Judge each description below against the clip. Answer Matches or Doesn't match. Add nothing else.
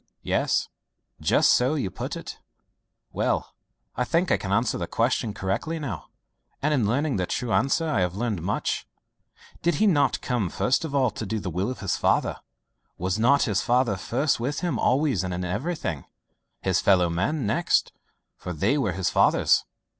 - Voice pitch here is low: Matches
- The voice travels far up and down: Matches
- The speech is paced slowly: Doesn't match